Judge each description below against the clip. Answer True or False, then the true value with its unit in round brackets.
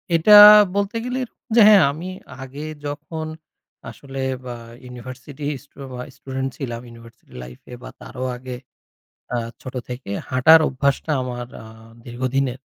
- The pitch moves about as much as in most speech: True (3.6 semitones)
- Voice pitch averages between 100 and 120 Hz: False (135 Hz)